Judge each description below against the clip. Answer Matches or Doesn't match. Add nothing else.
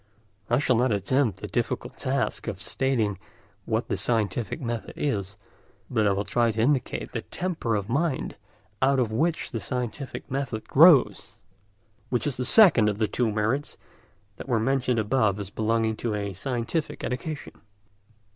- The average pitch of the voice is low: Matches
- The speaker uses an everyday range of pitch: Matches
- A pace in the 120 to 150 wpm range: Doesn't match